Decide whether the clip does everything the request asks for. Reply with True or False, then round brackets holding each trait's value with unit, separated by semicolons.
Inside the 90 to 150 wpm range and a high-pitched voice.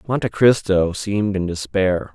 False (140 wpm; 100 Hz)